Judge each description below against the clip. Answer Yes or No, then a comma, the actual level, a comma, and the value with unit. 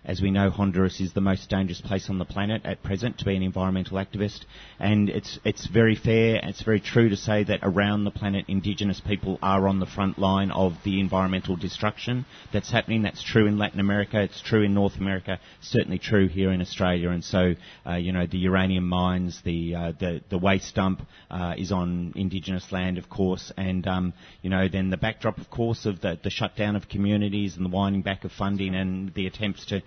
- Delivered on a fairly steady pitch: Yes, narrow, 1.6 semitones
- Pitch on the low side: Yes, very low, 95 Hz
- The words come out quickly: Yes, fast, 215 wpm